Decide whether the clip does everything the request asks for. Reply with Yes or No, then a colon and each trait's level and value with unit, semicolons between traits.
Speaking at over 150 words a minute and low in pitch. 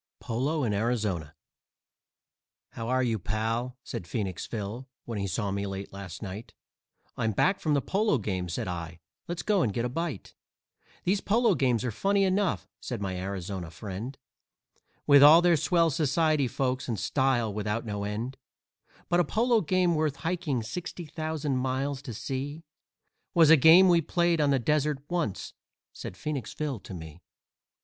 Yes: average, 165 wpm; low, 130 Hz